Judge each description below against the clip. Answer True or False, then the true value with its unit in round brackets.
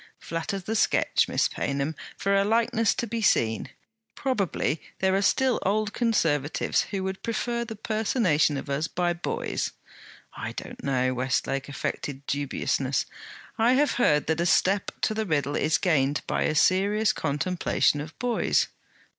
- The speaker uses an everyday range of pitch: False (7.0 semitones)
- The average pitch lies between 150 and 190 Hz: True (185 Hz)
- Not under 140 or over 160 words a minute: True (155 wpm)